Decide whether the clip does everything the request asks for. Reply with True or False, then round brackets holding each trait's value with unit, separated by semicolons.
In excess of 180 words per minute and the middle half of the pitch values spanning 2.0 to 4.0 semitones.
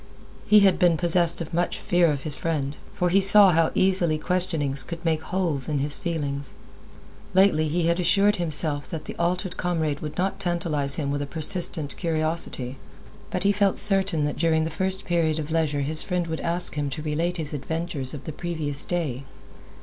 True (190 wpm; 3.1 semitones)